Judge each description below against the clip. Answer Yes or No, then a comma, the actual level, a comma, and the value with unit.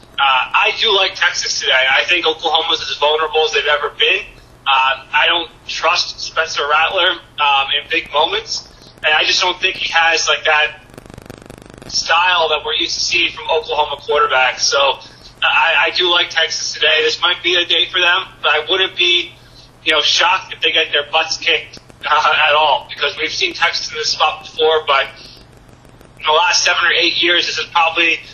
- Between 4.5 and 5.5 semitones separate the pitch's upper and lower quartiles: No, average, 2.7 semitones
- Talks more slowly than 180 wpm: No, average, 195 wpm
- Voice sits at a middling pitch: Yes, medium, 160 Hz